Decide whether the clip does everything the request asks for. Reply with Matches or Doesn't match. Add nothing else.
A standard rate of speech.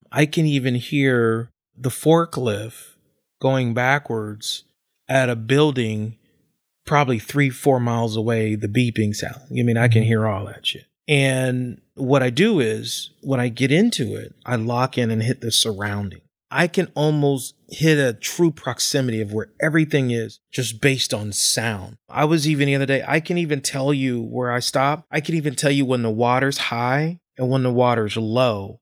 Matches